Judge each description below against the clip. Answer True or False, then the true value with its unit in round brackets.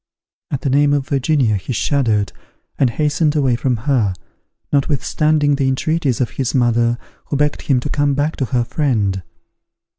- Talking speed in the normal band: True (160 wpm)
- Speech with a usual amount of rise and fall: True (3.4 semitones)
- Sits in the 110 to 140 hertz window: True (135 Hz)